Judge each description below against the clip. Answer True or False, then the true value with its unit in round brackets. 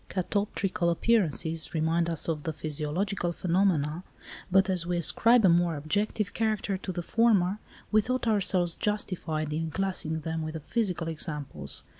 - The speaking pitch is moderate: True (175 Hz)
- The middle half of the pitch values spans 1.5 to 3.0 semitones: False (3.9 semitones)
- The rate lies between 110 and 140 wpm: False (150 wpm)